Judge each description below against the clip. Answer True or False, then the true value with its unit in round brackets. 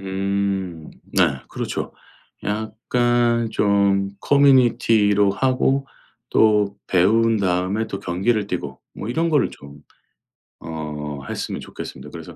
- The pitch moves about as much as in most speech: True (3.8 semitones)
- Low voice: True (100 Hz)